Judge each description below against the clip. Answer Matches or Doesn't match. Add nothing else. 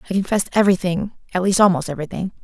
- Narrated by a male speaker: Doesn't match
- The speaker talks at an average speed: Matches